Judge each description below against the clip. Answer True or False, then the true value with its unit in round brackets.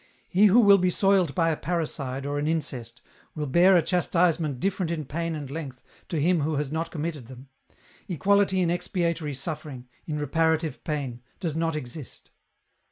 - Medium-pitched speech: True (160 Hz)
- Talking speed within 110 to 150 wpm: False (170 wpm)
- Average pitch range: True (3.5 semitones)